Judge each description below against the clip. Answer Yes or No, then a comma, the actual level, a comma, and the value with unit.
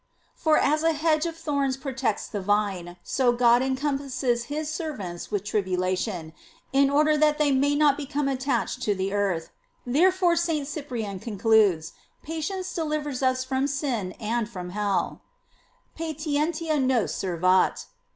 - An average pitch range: No, wide, 6.5 semitones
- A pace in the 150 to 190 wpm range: No, average, 140 wpm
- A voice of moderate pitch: No, very high, 265 Hz